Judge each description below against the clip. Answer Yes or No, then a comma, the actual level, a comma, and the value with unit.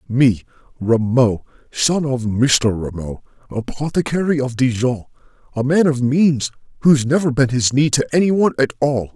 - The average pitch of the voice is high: No, low, 130 Hz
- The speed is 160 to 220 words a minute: No, average, 145 wpm